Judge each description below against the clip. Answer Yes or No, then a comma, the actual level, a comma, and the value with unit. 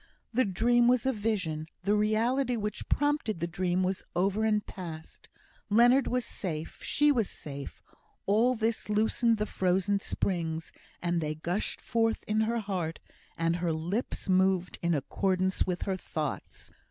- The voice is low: No, high, 195 Hz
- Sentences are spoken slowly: No, average, 155 wpm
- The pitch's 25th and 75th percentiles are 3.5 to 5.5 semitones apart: Yes, average, 4.5 semitones